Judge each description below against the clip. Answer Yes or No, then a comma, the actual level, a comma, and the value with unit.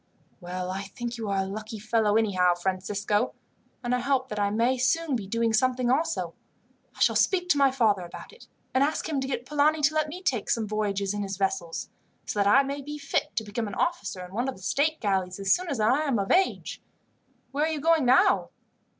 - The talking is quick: Yes, fast, 225 wpm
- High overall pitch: Yes, high, 230 Hz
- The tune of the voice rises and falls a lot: Yes, wide, 5.9 semitones